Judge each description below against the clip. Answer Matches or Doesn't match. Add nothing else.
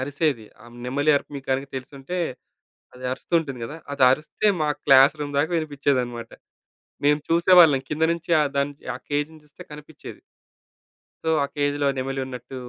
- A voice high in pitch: Doesn't match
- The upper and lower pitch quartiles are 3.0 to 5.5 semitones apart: Doesn't match